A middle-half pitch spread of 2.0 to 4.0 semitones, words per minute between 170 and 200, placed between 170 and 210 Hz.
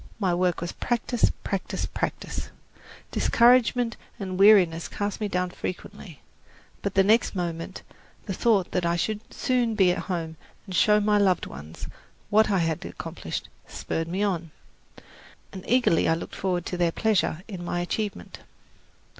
No: average, 3.4 semitones; average, 155 wpm; high, 190 Hz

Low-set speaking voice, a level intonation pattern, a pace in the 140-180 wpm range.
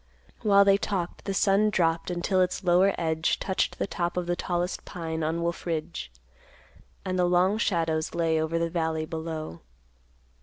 No: medium, 175 Hz; narrow, 2.3 semitones; average, 165 wpm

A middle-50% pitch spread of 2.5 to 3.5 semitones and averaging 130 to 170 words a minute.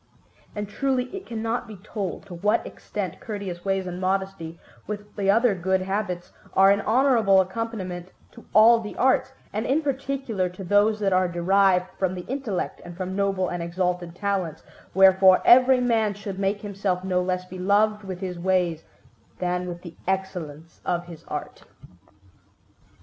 Yes: average, 2.8 semitones; average, 160 wpm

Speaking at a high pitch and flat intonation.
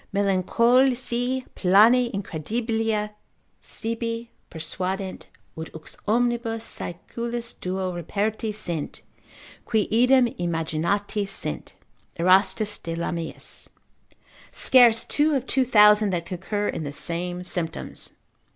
No: high, 210 Hz; average, 4.6 semitones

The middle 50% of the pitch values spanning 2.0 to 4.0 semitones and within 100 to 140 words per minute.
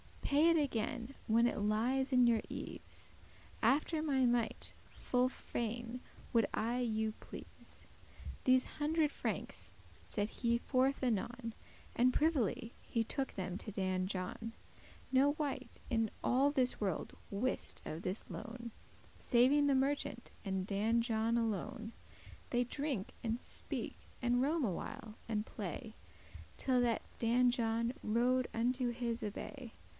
Yes: average, 2.8 semitones; slow, 135 wpm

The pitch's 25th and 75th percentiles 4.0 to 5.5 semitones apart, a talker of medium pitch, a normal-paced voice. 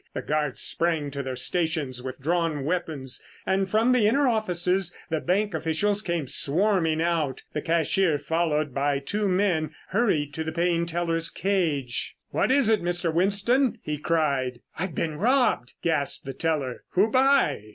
Yes: average, 4.7 semitones; medium, 165 Hz; average, 160 wpm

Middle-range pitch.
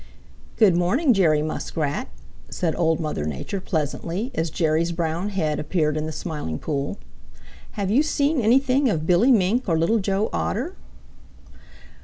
Yes: medium, 175 Hz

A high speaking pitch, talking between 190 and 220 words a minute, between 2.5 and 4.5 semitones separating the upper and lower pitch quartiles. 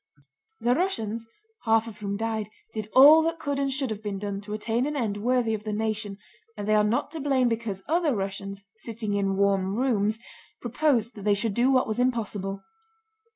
Yes: high, 220 Hz; average, 200 wpm; average, 3.6 semitones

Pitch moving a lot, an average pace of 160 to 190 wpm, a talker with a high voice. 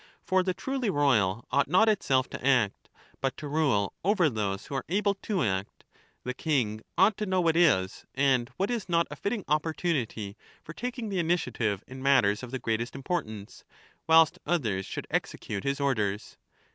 No: wide, 8.1 semitones; average, 175 wpm; medium, 140 Hz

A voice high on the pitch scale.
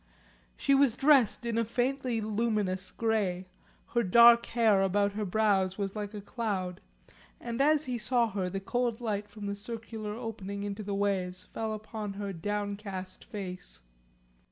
Yes: high, 210 Hz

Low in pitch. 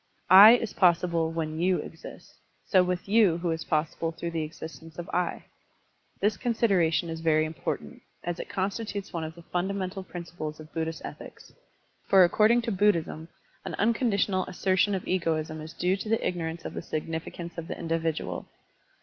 No: medium, 175 Hz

